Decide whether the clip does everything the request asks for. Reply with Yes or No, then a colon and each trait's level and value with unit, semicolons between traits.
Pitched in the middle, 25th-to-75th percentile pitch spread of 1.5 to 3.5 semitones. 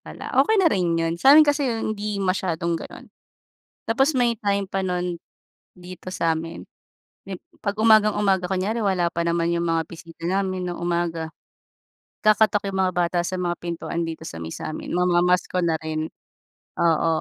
Yes: medium, 180 Hz; average, 3.2 semitones